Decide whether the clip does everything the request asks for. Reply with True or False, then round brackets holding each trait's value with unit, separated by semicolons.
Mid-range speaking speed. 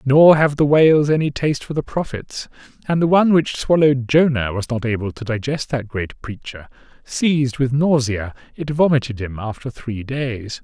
True (180 wpm)